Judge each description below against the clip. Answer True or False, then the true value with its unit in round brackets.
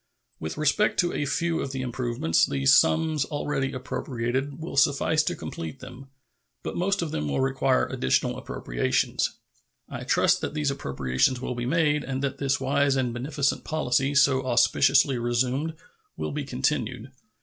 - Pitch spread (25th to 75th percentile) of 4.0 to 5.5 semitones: False (2.9 semitones)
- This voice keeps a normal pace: True (160 wpm)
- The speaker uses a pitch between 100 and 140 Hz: True (135 Hz)